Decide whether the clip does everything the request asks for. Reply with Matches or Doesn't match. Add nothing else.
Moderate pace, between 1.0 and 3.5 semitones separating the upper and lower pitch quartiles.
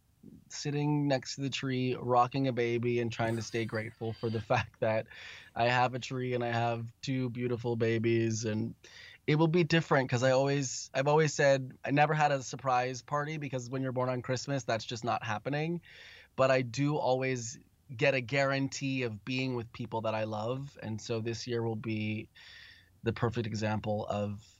Matches